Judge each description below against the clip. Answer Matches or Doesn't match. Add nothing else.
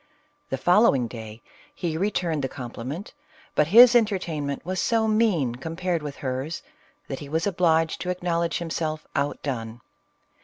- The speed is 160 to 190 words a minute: Doesn't match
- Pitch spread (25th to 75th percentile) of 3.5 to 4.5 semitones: Doesn't match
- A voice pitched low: Doesn't match